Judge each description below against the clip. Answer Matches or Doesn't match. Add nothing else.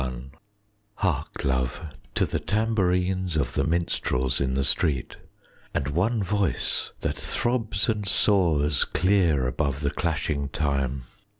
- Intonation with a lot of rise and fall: Matches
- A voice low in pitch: Matches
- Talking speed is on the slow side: Matches